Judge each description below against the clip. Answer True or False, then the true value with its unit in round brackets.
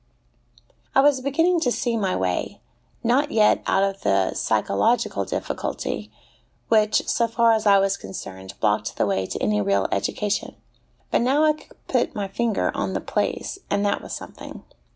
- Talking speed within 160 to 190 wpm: True (170 wpm)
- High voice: True (205 Hz)